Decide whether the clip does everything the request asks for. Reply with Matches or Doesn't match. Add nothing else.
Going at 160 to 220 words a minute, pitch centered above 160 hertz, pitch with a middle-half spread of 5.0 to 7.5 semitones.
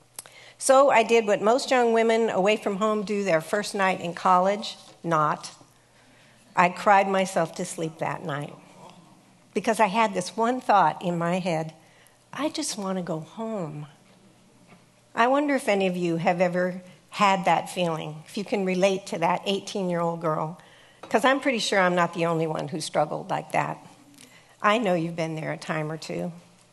Doesn't match